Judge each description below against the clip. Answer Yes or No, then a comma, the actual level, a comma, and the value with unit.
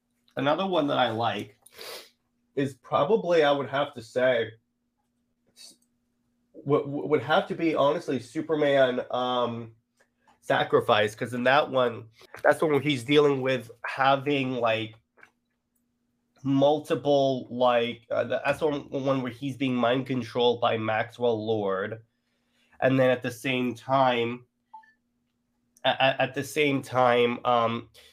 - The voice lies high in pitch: No, low, 125 Hz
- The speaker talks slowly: Yes, slow, 125 wpm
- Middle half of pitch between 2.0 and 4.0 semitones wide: Yes, average, 2.7 semitones